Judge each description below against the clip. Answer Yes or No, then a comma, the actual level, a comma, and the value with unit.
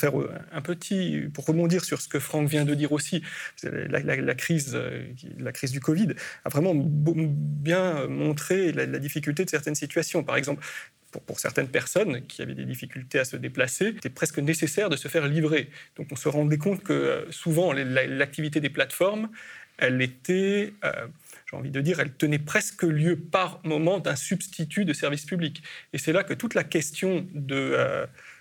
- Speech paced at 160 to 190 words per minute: Yes, average, 185 wpm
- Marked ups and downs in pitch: No, average, 3.5 semitones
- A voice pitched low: No, medium, 155 Hz